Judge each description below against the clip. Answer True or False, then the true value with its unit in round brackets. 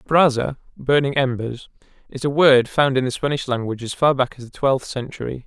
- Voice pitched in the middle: False (130 Hz)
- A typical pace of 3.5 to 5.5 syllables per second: True (5.3 syllables/s)